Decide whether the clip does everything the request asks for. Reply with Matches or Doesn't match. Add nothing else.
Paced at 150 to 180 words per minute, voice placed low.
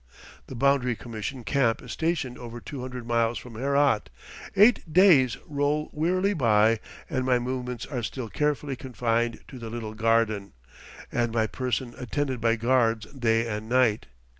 Matches